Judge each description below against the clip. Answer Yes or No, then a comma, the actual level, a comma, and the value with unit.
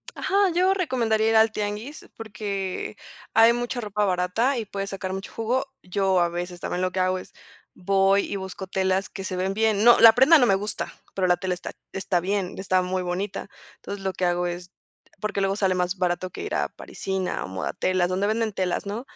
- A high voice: Yes, high, 195 Hz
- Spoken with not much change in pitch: No, average, 3.0 semitones